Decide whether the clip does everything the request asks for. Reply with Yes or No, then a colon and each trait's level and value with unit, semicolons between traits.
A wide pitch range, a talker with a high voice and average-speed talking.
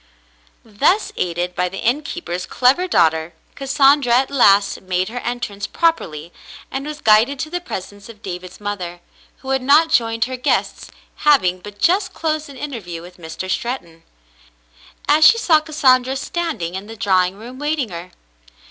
Yes: wide, 7.5 semitones; high, 230 Hz; average, 165 wpm